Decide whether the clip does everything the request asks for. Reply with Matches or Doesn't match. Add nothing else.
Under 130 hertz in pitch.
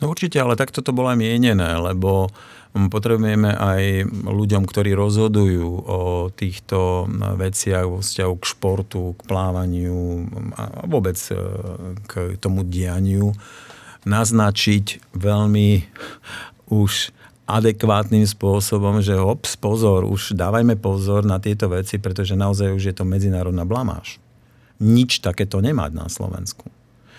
Matches